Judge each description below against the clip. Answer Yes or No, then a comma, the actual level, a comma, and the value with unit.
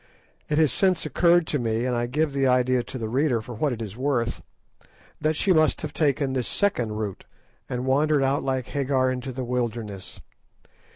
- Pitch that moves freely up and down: No, average, 3.7 semitones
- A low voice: Yes, low, 130 Hz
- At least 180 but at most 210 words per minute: Yes, average, 190 wpm